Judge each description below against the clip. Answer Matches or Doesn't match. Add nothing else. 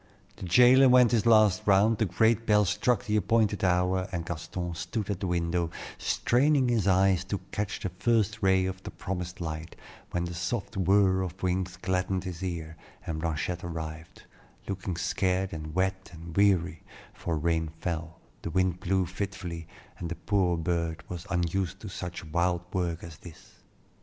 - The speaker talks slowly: Doesn't match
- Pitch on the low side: Matches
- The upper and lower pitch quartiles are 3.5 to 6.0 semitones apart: Doesn't match